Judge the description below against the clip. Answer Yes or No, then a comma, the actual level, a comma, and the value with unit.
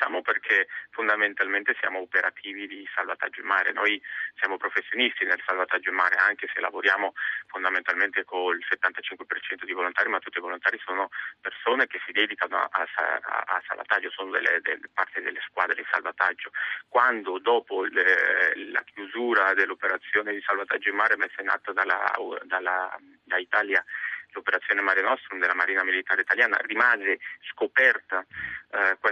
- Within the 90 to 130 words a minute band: No, average, 145 wpm